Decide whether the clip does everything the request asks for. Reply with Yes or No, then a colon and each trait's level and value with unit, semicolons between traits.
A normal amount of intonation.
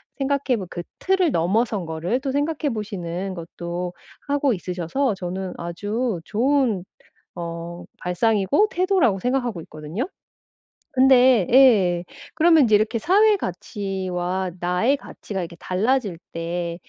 No: wide, 6.9 semitones